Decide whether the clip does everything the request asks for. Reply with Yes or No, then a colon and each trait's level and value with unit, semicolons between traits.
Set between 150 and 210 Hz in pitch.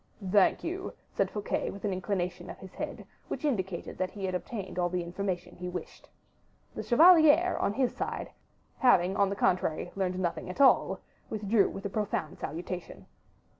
Yes: high, 190 Hz